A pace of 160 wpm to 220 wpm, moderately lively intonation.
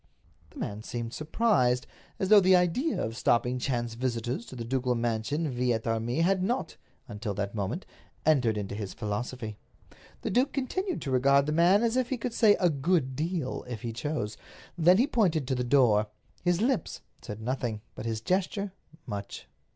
No: average, 180 wpm; wide, 7.8 semitones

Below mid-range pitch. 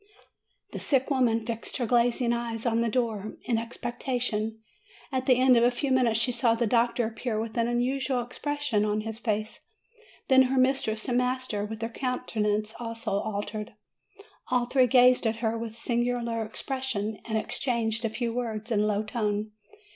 No: high, 235 Hz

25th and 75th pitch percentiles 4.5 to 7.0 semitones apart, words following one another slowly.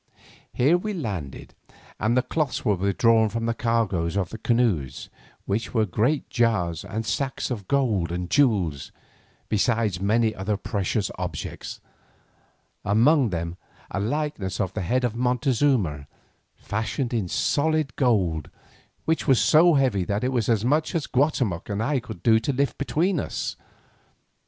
No: average, 5.1 semitones; average, 150 wpm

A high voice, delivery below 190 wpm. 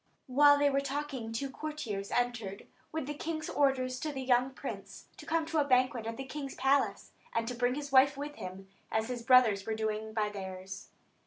No: very high, 255 Hz; average, 195 wpm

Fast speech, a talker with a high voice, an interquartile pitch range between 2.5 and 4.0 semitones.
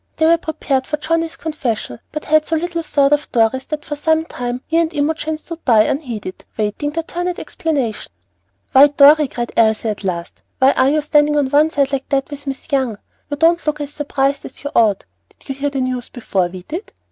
Yes: fast, 215 wpm; very high, 285 Hz; average, 3.6 semitones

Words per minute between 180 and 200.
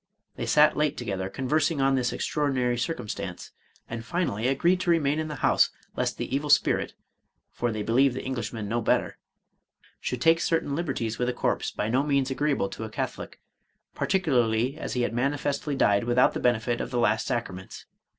Yes: average, 190 wpm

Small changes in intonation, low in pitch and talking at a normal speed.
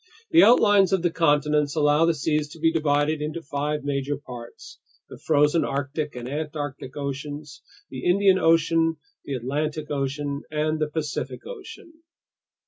No: narrow, 2.2 semitones; medium, 150 Hz; average, 145 wpm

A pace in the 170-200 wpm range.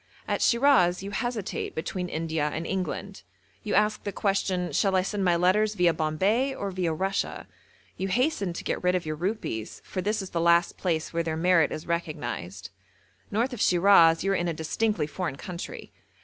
Yes: average, 190 wpm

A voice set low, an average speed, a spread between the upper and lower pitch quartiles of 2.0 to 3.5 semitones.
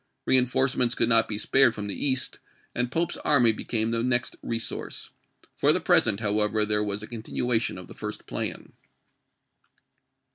Yes: low, 115 Hz; average, 155 wpm; average, 2.7 semitones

